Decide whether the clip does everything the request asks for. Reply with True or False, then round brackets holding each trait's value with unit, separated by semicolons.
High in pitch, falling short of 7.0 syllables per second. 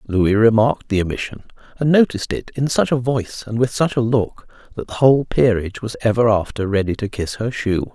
False (115 Hz; 5.9 syllables/s)